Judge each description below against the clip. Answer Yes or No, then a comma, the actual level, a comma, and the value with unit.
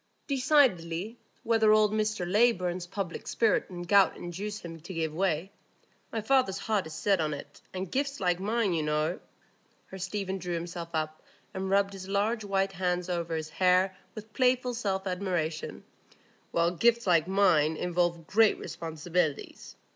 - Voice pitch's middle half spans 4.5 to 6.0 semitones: No, average, 3.6 semitones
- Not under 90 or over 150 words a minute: Yes, average, 145 wpm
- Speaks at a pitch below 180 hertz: No, medium, 185 Hz